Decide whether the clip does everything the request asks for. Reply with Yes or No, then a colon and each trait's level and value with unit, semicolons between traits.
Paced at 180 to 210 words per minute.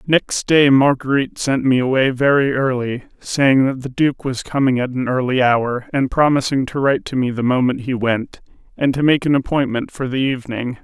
Yes: average, 200 wpm